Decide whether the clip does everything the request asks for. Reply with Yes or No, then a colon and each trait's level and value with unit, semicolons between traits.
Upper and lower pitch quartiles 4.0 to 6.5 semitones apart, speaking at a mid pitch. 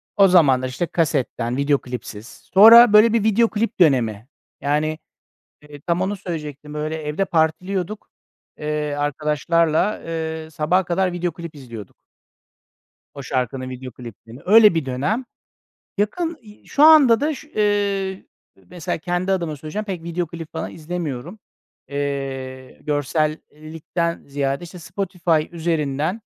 Yes: average, 4.8 semitones; medium, 160 Hz